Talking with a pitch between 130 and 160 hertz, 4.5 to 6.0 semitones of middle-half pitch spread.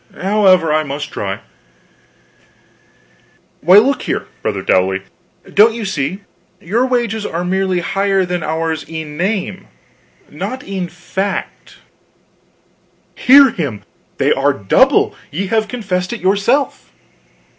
No: medium, 185 Hz; average, 4.8 semitones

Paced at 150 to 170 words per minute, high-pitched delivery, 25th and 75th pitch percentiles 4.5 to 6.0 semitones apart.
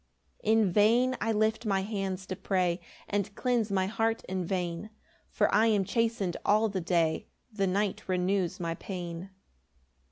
No: average, 160 wpm; high, 195 Hz; average, 2.9 semitones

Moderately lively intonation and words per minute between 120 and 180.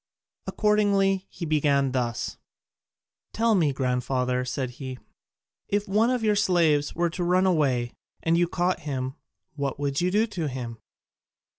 No: wide, 6.6 semitones; average, 145 wpm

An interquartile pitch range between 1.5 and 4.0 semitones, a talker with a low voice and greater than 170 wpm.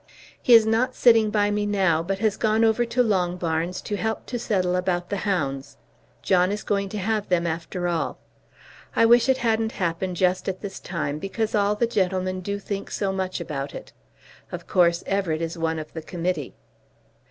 No: average, 3.5 semitones; high, 190 Hz; average, 190 wpm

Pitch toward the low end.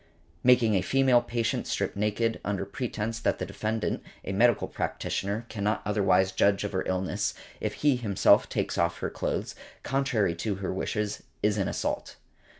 Yes: low, 105 Hz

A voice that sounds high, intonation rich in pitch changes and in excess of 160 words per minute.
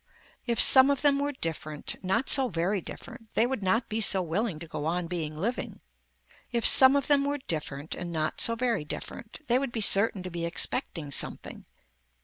Yes: high, 210 Hz; wide, 7.2 semitones; average, 195 wpm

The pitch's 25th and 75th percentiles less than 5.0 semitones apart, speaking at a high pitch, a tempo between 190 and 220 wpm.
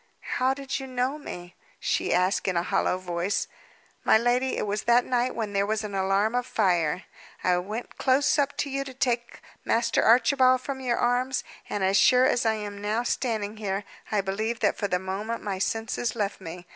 Yes: average, 4.3 semitones; high, 220 Hz; average, 200 wpm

